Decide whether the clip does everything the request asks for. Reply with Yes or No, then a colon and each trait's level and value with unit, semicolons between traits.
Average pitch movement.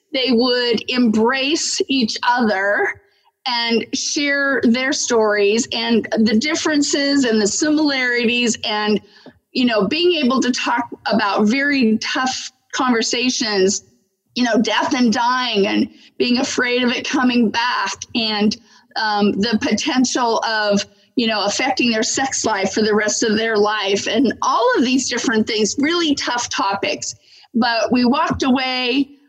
Yes: average, 4.0 semitones